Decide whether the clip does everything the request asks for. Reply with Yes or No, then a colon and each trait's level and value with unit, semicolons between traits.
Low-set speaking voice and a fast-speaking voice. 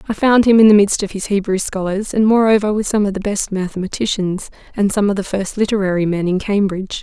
No: high, 200 Hz; fast, 230 wpm